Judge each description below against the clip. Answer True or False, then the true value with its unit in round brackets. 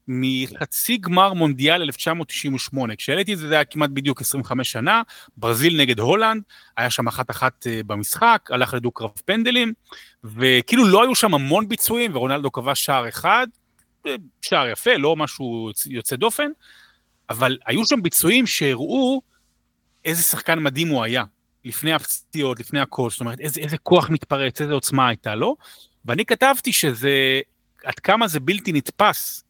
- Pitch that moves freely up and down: True (7.1 semitones)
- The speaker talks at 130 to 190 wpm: True (150 wpm)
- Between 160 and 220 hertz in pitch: False (145 Hz)